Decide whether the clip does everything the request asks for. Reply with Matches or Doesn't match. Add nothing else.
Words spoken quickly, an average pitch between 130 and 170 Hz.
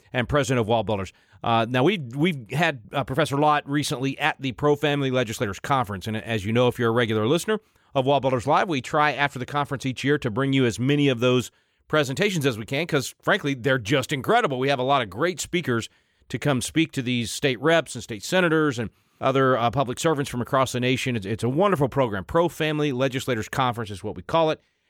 Matches